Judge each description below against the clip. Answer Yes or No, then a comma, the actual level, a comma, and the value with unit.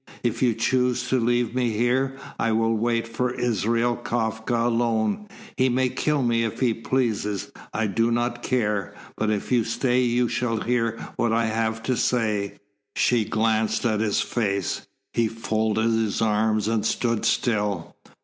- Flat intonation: Yes, narrow, 1.8 semitones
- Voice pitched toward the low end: Yes, low, 115 Hz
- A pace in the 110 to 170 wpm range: Yes, average, 160 wpm